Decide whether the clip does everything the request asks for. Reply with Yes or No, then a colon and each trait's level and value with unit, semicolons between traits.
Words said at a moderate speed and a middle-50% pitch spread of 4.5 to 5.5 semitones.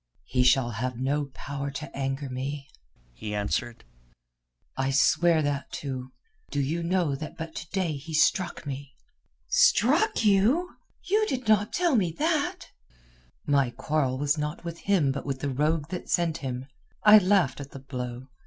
Yes: average, 160 wpm; average, 5.2 semitones